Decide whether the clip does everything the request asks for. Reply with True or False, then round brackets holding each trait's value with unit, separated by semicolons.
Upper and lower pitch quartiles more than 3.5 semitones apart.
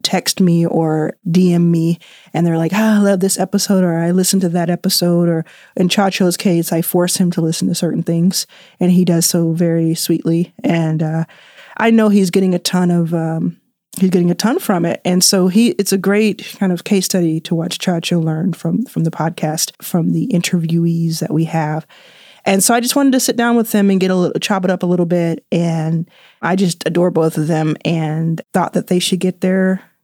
False (2.6 semitones)